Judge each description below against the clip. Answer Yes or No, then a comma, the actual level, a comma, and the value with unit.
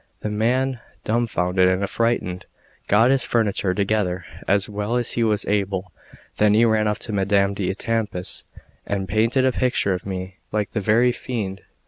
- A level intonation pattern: No, average, 3.0 semitones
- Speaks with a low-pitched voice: Yes, low, 105 Hz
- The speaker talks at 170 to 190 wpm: No, average, 160 wpm